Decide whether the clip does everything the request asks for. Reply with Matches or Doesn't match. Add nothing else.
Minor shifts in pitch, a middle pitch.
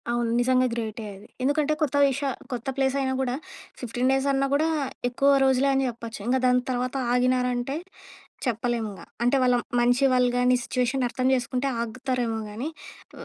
Doesn't match